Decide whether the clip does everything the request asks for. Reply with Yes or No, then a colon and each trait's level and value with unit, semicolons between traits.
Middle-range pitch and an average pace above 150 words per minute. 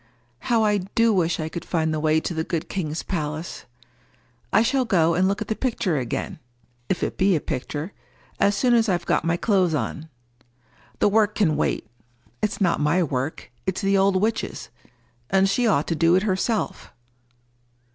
Yes: medium, 180 Hz; average, 175 wpm